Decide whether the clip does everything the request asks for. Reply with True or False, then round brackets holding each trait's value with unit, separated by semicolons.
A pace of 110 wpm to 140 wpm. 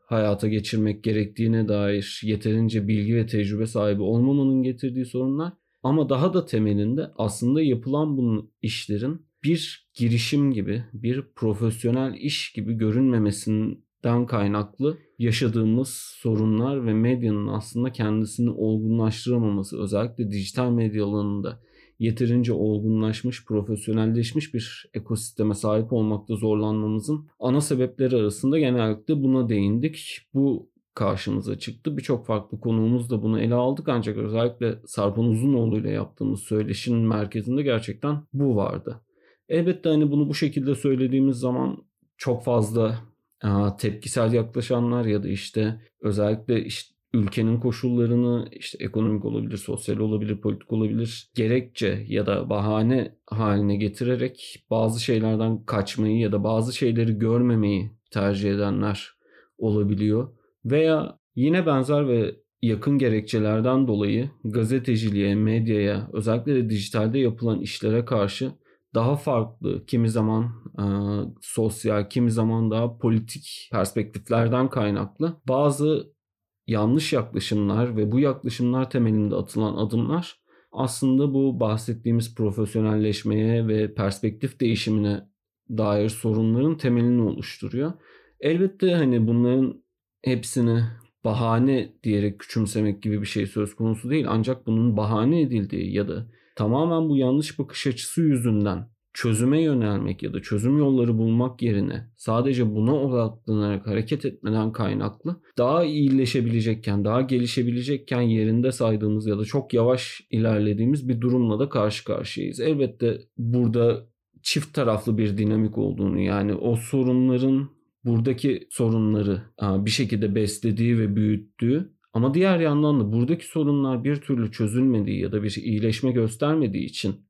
True (120 wpm)